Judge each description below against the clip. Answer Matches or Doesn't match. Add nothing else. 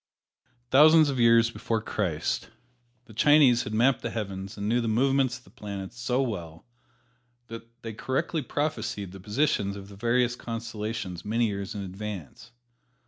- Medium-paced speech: Matches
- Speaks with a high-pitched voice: Doesn't match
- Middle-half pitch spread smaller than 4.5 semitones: Matches